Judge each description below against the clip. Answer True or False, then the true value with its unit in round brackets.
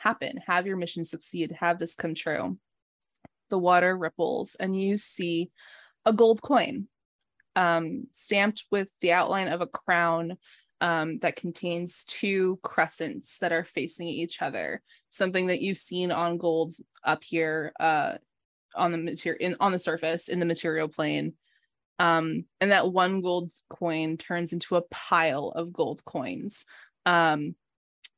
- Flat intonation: True (2.0 semitones)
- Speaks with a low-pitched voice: False (175 Hz)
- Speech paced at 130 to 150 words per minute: True (145 wpm)